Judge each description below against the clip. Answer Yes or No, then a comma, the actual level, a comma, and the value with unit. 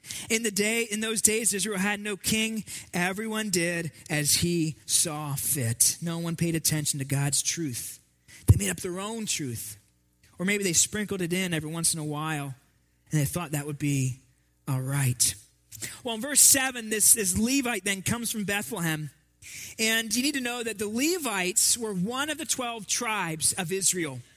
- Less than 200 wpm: Yes, average, 185 wpm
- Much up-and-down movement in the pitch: Yes, wide, 7.3 semitones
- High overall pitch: No, medium, 175 Hz